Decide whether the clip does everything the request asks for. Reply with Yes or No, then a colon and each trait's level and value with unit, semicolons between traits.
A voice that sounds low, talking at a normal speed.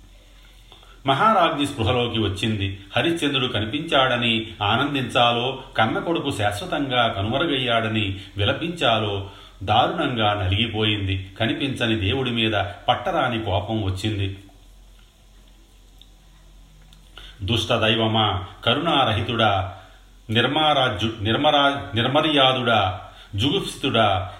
No: low, 110 Hz; slow, 60 wpm